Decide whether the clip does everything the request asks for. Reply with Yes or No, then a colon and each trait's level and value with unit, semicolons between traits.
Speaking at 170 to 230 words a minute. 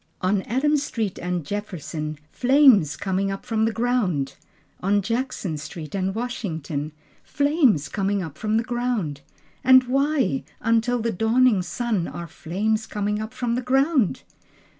No: average, 140 wpm